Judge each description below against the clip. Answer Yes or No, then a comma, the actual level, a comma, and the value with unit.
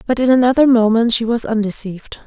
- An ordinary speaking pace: Yes, average, 185 wpm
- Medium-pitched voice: No, high, 230 Hz